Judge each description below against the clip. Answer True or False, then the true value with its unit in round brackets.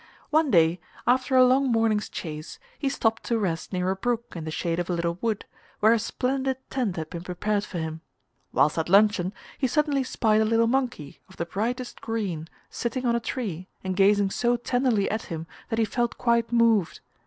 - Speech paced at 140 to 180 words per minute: False (200 wpm)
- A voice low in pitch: False (220 Hz)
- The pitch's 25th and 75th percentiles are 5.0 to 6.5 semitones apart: True (5.3 semitones)